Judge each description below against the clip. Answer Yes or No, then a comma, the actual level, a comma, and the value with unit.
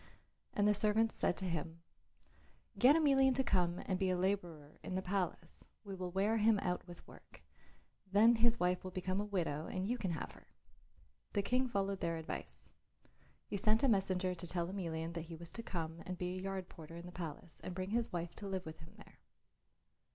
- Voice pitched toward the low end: No, medium, 185 Hz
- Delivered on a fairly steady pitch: No, average, 3.2 semitones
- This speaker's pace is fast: Yes, fast, 210 wpm